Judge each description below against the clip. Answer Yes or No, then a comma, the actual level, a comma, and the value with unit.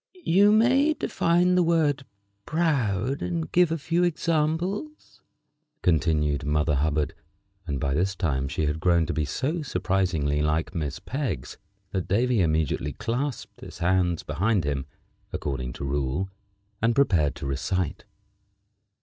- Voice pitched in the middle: No, very low, 95 Hz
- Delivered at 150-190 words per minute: No, slow, 135 wpm